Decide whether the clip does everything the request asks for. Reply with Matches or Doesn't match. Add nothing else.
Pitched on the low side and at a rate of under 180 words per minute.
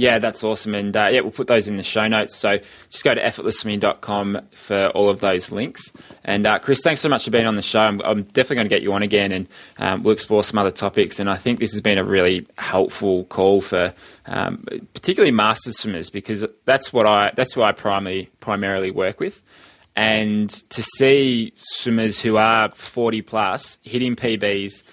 Doesn't match